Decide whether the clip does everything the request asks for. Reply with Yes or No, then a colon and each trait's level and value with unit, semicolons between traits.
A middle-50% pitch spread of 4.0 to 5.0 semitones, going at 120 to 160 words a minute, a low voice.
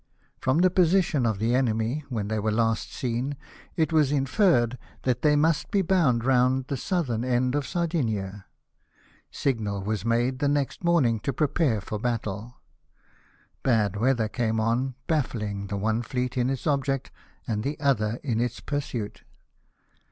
Yes: average, 4.4 semitones; average, 155 wpm; low, 125 Hz